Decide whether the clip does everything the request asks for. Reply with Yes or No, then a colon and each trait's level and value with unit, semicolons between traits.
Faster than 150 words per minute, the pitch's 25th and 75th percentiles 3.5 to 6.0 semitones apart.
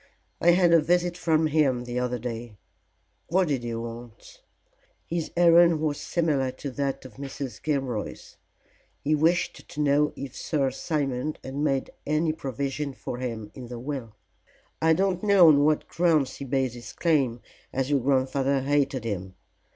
Yes: average, 160 wpm; average, 3.8 semitones